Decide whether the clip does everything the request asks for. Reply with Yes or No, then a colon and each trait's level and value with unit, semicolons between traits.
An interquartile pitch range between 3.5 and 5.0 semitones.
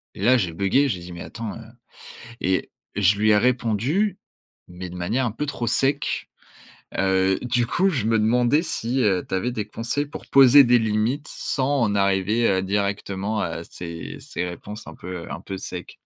Yes: average, 4.6 semitones